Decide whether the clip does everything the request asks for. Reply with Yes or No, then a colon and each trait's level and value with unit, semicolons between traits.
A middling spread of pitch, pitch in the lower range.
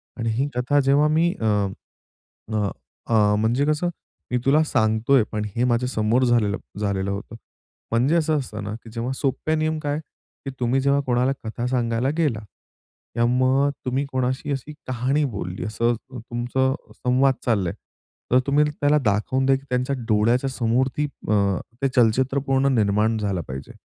Yes: average, 3.7 semitones; low, 125 Hz